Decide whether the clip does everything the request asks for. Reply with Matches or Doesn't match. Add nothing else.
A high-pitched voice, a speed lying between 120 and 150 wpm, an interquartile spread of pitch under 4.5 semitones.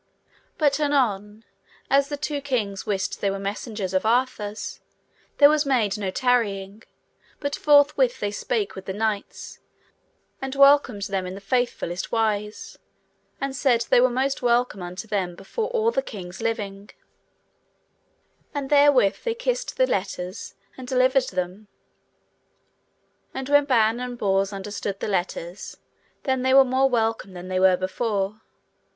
Doesn't match